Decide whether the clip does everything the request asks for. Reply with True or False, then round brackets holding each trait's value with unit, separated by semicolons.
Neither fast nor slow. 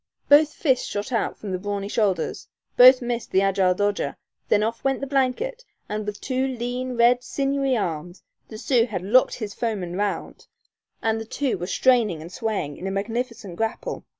True (180 wpm)